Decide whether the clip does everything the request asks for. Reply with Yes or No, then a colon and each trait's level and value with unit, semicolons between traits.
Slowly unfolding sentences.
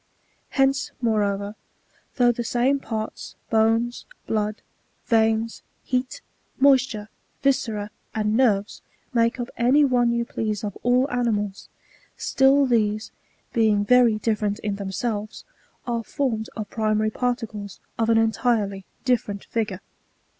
Yes: slow, 120 wpm